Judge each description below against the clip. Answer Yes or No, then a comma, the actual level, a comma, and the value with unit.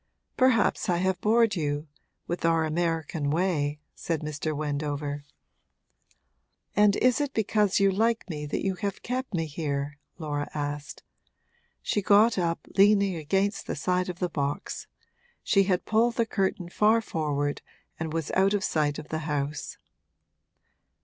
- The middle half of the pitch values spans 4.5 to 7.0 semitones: Yes, average, 5.2 semitones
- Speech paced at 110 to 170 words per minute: Yes, average, 150 wpm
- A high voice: No, medium, 170 Hz